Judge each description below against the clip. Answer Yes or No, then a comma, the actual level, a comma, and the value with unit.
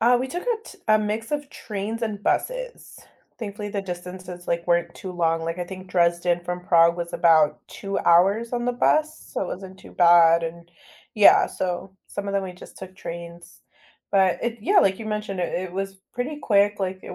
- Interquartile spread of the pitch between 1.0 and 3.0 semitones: No, average, 3.7 semitones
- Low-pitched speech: No, high, 190 Hz